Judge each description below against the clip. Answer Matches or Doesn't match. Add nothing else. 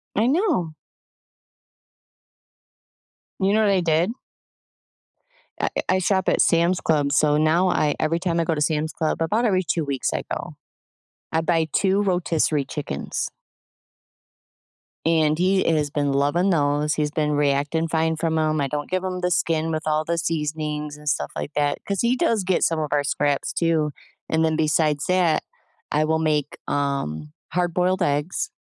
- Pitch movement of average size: Matches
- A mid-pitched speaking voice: Matches